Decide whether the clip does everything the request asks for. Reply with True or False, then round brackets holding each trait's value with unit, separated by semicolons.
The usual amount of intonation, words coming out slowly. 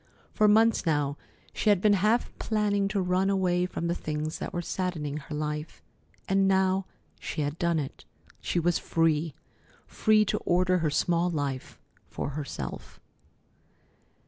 False (4.1 semitones; 150 wpm)